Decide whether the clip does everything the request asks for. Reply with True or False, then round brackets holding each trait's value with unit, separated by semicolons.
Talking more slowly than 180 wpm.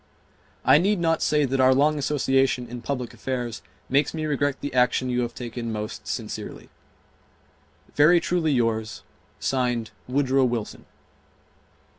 True (135 wpm)